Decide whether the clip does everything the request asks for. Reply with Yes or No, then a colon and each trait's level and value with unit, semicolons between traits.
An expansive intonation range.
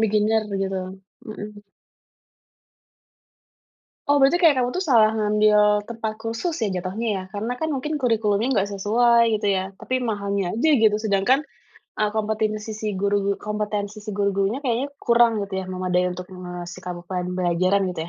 No: average, 2.7 semitones